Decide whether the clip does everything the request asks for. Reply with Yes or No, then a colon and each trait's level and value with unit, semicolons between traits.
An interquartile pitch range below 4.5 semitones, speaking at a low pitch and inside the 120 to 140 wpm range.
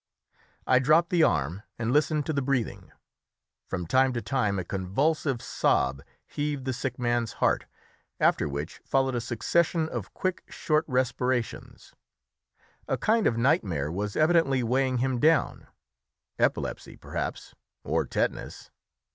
No: average, 4.8 semitones; low, 130 Hz; slow, 135 wpm